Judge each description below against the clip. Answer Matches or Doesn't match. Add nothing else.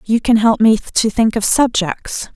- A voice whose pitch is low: Doesn't match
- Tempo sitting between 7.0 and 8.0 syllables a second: Doesn't match